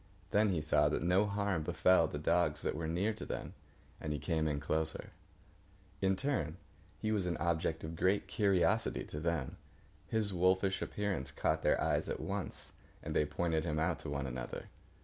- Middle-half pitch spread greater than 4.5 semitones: No, average, 3.9 semitones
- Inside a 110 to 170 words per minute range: No, average, 185 wpm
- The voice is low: Yes, very low, 85 Hz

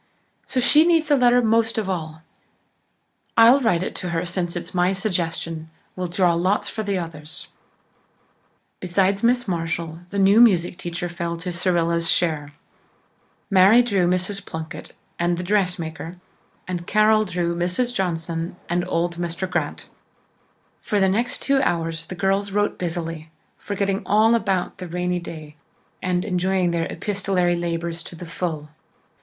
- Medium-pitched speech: Yes, medium, 180 Hz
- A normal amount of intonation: Yes, average, 3.0 semitones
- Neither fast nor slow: Yes, average, 150 wpm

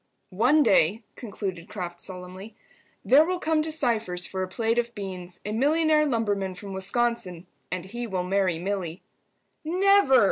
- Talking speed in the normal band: Yes, average, 150 wpm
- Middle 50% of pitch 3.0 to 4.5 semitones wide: No, wide, 5.6 semitones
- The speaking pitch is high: Yes, high, 205 Hz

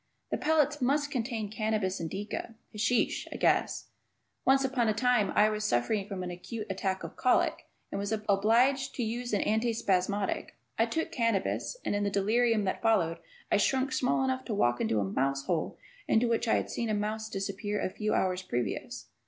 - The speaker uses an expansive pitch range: No, average, 3.8 semitones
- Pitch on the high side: Yes, high, 215 Hz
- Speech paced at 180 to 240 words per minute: Yes, average, 190 wpm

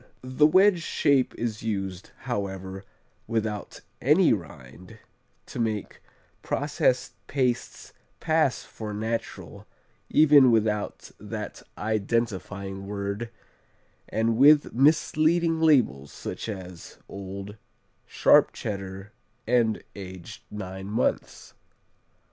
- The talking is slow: Yes, slow, 90 wpm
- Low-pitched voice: Yes, low, 110 Hz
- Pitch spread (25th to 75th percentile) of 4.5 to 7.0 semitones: Yes, average, 5.1 semitones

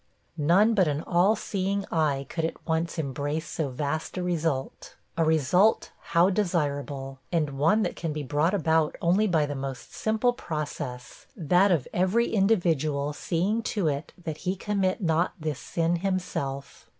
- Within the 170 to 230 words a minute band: No, average, 160 wpm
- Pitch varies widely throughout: No, average, 4.1 semitones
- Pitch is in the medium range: Yes, medium, 165 Hz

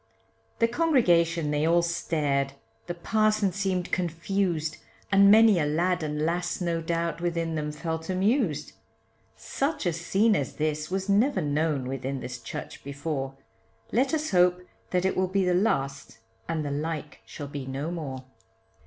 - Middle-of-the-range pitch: Yes, medium, 170 Hz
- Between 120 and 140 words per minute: No, average, 155 wpm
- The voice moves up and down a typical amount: Yes, average, 4.1 semitones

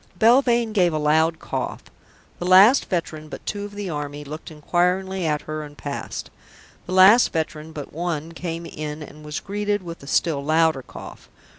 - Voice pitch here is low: No, medium, 165 Hz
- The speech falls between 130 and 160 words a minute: No, average, 175 wpm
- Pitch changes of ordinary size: Yes, average, 3.7 semitones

